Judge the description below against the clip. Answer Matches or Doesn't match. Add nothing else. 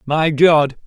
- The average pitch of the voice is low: Doesn't match